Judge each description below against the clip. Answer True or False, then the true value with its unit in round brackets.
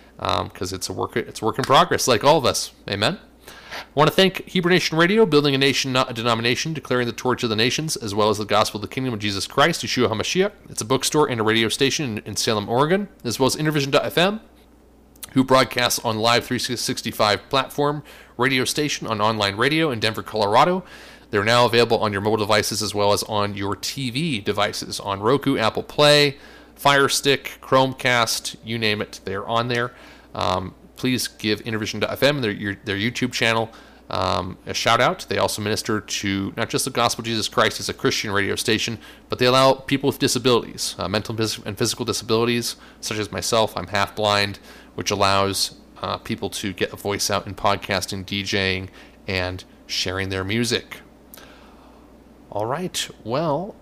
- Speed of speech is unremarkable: True (185 wpm)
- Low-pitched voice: True (115 Hz)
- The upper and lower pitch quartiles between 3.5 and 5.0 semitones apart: True (4.2 semitones)